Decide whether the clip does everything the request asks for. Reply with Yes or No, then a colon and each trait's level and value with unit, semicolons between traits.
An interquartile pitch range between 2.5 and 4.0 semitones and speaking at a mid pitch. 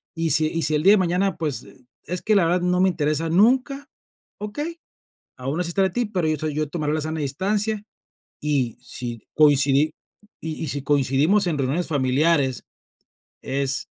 No: average, 4.6 semitones; medium, 160 Hz